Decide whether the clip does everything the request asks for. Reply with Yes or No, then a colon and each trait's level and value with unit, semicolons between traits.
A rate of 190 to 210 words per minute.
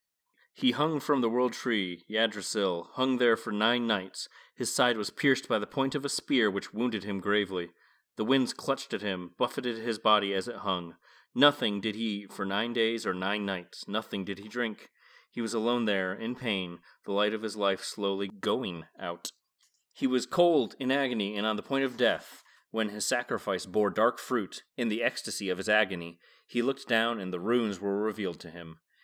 Yes: average, 200 wpm